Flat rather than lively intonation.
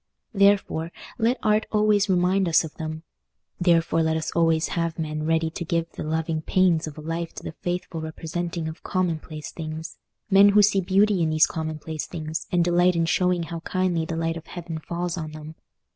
Yes: narrow, 2.2 semitones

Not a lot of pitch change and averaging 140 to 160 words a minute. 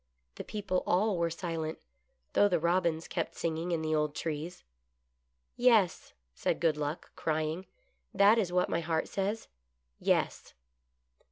No: average, 3.0 semitones; average, 145 wpm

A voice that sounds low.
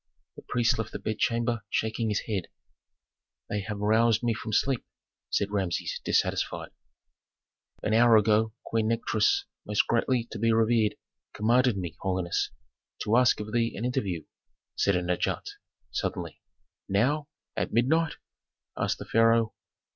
Yes: low, 110 Hz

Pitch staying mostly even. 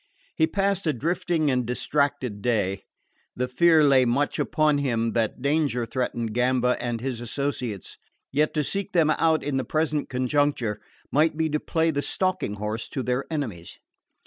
No: average, 4.3 semitones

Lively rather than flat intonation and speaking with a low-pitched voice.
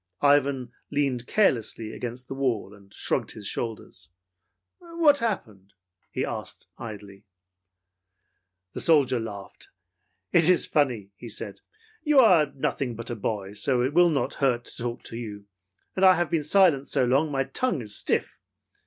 Yes: wide, 5.7 semitones; low, 130 Hz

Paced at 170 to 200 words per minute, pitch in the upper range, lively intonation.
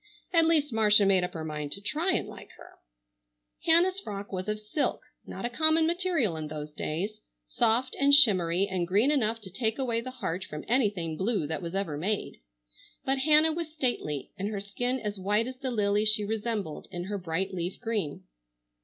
Yes: average, 195 wpm; high, 210 Hz; wide, 5.9 semitones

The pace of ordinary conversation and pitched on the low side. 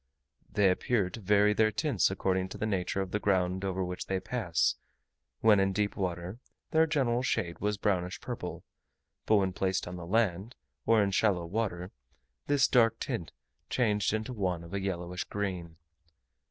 Yes: average, 170 wpm; low, 100 Hz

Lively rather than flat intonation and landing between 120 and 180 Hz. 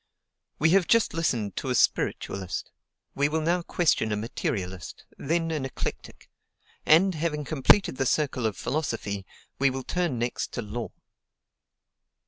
Yes: wide, 6.1 semitones; low, 135 Hz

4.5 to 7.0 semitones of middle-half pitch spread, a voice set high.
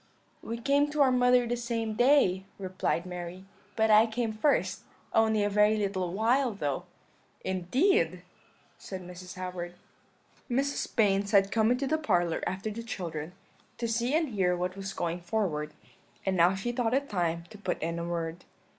Yes: average, 4.9 semitones; high, 205 Hz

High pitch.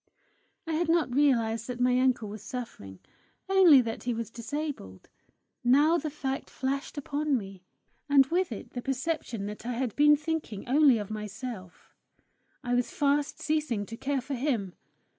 Yes: very high, 255 Hz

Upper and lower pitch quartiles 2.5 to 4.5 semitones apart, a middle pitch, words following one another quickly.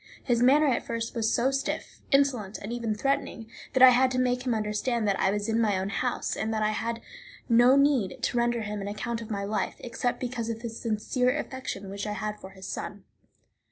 No: average, 3.0 semitones; high, 230 Hz; fast, 225 wpm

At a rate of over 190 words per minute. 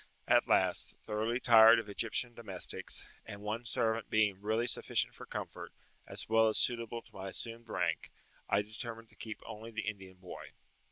No: average, 170 wpm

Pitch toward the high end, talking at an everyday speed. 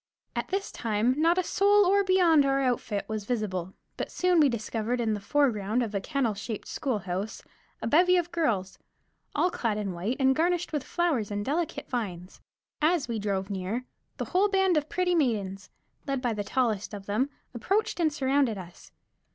Yes: high, 245 Hz; average, 180 wpm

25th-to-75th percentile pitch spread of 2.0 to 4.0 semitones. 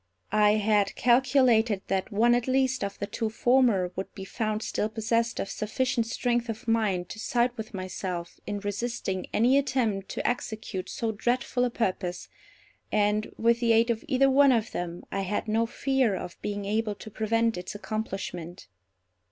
Yes: average, 3.1 semitones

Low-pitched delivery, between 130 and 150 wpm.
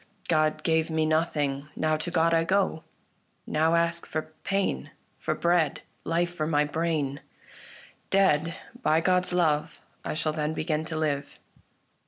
No: medium, 160 Hz; average, 145 wpm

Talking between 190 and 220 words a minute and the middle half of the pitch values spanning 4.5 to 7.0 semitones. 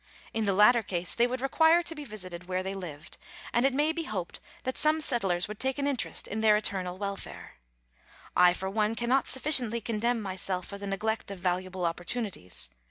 Yes: average, 195 wpm; average, 5.0 semitones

